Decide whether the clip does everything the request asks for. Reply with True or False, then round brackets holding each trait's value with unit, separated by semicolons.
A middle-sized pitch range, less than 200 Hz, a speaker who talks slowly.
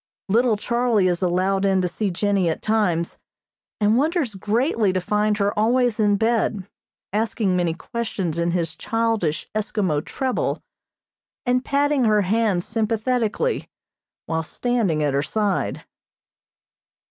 False (4.0 semitones; 210 Hz; 130 wpm)